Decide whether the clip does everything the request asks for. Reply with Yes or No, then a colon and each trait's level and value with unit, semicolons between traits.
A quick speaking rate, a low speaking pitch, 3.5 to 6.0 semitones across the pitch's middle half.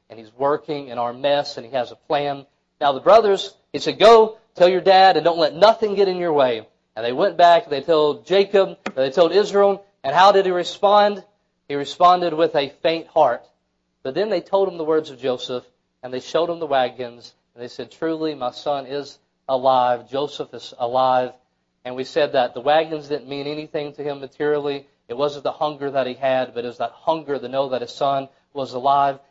No: fast, 220 wpm; medium, 145 Hz; average, 4.6 semitones